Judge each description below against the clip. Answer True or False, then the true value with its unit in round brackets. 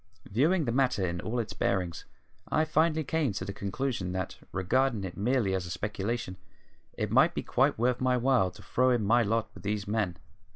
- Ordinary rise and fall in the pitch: True (5.0 semitones)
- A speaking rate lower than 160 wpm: False (200 wpm)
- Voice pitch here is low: True (110 Hz)